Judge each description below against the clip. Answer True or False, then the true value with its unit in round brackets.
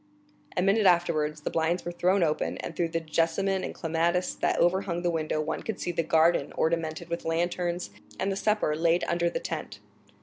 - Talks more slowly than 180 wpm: False (195 wpm)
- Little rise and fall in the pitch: True (1.6 semitones)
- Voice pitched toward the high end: False (170 Hz)